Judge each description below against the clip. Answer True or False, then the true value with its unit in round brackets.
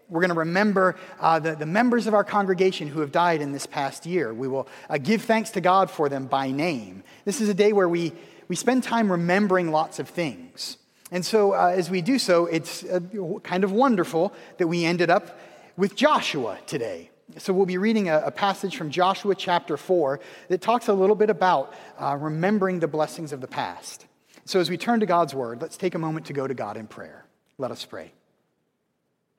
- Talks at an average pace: False (215 wpm)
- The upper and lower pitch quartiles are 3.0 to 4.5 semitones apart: True (3.8 semitones)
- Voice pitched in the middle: True (180 Hz)